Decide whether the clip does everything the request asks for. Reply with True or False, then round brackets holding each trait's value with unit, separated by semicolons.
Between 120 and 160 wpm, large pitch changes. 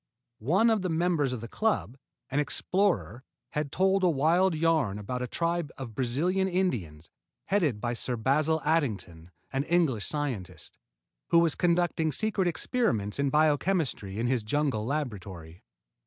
True (145 wpm; 6.8 semitones)